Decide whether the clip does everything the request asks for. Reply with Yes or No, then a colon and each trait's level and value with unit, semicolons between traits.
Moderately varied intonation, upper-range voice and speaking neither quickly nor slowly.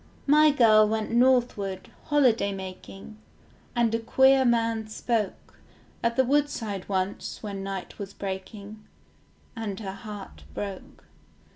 No: average, 3.3 semitones; high, 215 Hz; slow, 120 wpm